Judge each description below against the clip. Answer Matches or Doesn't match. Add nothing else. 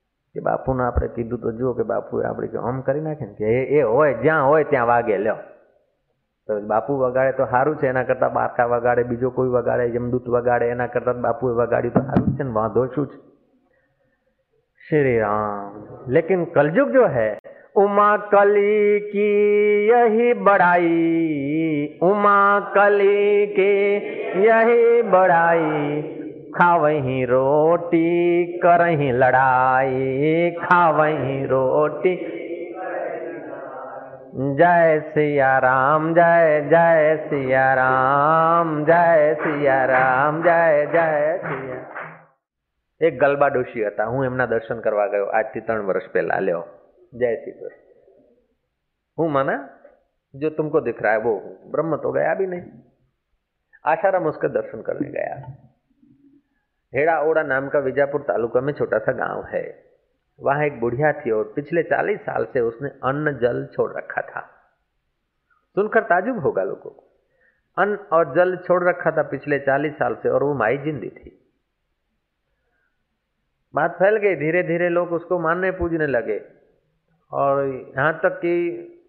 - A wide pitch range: Matches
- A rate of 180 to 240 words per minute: Doesn't match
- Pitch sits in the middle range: Matches